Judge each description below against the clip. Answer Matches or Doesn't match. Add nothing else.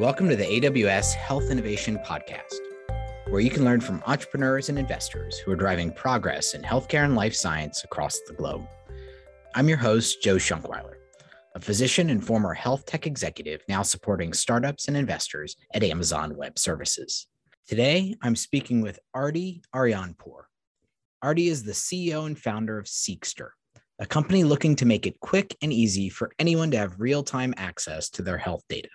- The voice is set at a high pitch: Doesn't match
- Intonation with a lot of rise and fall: Matches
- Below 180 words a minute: Matches